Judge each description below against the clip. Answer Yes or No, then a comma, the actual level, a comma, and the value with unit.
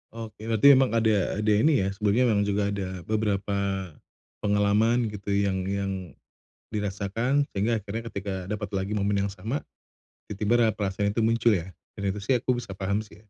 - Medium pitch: No, low, 105 Hz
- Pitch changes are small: Yes, narrow, 2.1 semitones